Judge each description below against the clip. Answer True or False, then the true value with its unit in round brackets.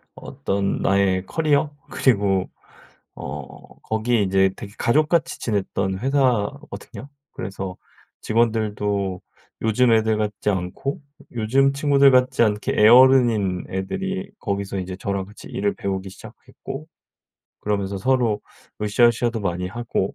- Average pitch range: True (4.6 semitones)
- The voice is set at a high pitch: False (105 Hz)